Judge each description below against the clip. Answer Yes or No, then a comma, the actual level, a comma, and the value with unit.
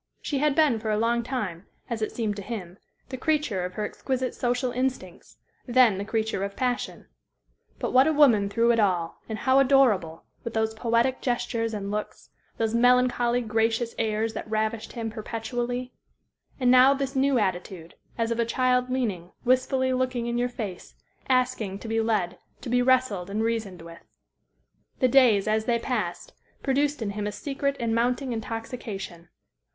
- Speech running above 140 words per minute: Yes, average, 175 wpm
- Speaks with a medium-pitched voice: No, high, 230 Hz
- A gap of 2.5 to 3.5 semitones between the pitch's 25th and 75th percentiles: Yes, average, 3.0 semitones